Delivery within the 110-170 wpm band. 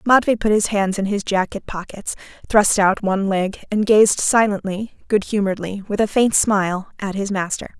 No: average, 185 wpm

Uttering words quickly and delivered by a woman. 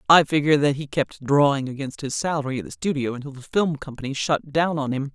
Yes: fast, 235 wpm; female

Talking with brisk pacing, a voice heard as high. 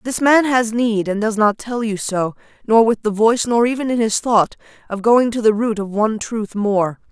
Yes: fast, 235 wpm; high, 220 Hz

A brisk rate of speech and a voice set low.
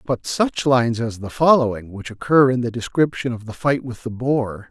Yes: fast, 215 wpm; low, 120 Hz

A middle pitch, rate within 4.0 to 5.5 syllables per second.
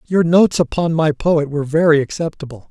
No: medium, 155 Hz; 5.9 syllables/s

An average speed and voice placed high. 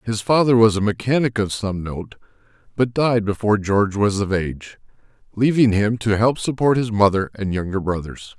No: average, 180 wpm; low, 105 Hz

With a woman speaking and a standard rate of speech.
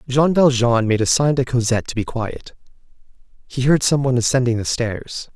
No: male; average, 190 wpm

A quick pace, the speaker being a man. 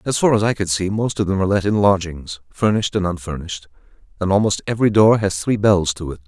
Yes: fast, 240 wpm; male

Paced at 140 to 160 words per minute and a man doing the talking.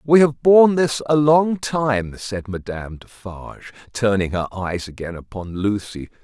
Yes: average, 155 wpm; male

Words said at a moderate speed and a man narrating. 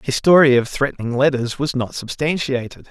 Yes: average, 165 wpm; male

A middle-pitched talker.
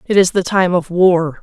Yes: medium, 180 Hz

